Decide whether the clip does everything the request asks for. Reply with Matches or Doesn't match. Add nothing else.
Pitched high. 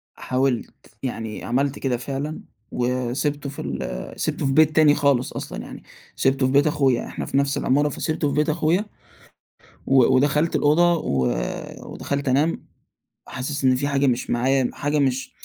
Doesn't match